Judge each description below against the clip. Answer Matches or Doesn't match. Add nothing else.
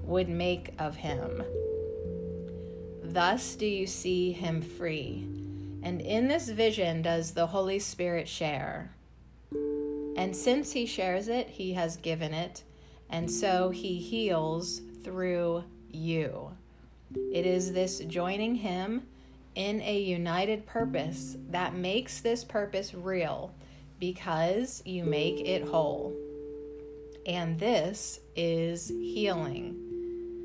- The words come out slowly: Matches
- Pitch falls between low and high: Matches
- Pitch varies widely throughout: Doesn't match